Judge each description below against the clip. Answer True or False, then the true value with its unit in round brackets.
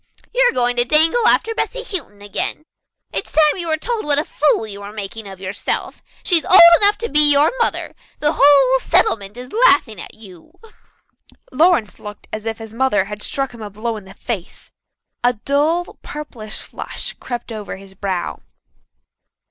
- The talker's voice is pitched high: True (245 Hz)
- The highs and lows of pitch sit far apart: True (6.6 semitones)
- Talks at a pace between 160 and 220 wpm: True (180 wpm)